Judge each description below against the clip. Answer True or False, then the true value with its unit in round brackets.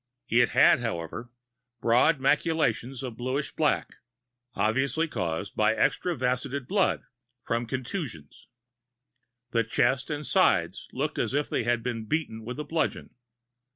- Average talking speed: False (125 wpm)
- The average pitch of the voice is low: True (125 Hz)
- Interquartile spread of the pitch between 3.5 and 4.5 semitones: True (4.2 semitones)